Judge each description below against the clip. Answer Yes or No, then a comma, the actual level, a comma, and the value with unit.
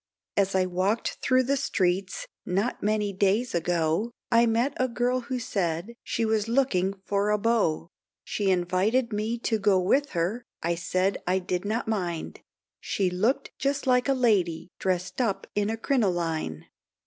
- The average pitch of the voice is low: No, high, 205 Hz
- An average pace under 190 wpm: Yes, average, 160 wpm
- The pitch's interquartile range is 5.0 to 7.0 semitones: No, average, 4.5 semitones